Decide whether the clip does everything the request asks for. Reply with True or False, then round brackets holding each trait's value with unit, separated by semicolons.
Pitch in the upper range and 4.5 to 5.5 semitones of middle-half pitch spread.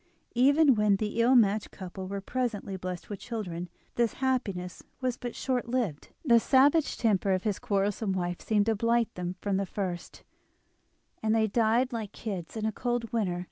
False (215 Hz; 3.7 semitones)